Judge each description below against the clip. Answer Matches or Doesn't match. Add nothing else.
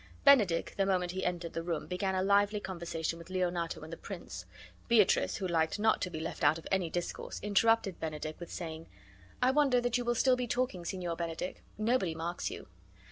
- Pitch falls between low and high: Matches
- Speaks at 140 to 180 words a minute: Doesn't match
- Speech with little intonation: Doesn't match